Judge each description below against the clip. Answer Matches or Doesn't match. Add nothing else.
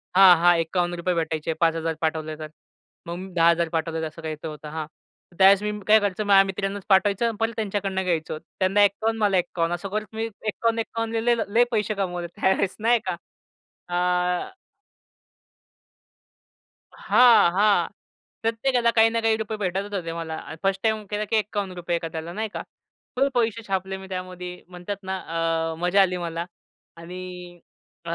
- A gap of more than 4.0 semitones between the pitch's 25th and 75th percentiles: Doesn't match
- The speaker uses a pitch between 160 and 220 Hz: Matches